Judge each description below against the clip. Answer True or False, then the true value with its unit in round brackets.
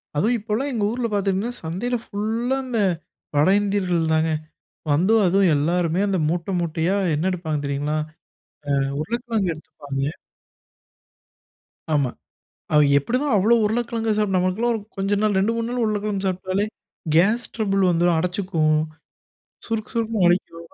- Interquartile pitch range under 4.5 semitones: False (4.9 semitones)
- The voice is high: True (195 Hz)